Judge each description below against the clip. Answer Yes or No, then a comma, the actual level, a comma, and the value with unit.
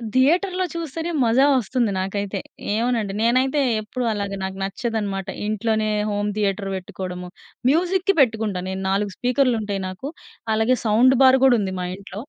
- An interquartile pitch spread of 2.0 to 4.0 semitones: No, average, 4.7 semitones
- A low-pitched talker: No, high, 220 Hz